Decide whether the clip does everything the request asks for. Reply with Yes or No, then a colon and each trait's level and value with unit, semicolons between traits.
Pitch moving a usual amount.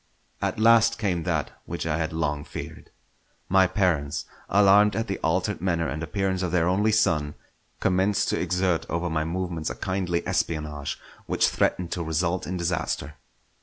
Yes: average, 3.2 semitones